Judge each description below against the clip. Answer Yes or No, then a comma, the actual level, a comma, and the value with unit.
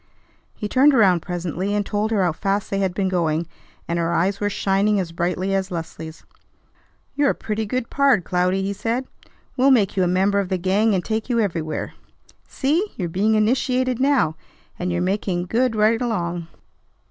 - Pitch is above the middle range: Yes, high, 195 Hz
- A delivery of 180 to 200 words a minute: Yes, average, 185 wpm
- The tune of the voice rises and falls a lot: No, average, 3.9 semitones